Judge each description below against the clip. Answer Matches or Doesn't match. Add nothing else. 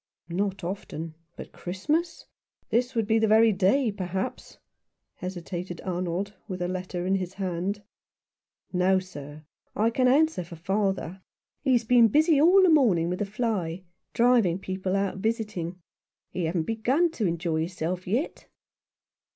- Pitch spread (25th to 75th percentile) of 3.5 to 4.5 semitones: Matches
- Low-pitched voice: Doesn't match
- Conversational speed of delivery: Matches